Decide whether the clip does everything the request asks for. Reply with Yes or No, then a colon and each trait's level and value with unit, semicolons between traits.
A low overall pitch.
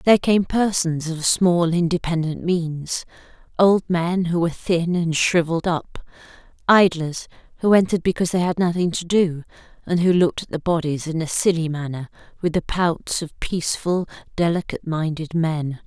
No: medium, 170 Hz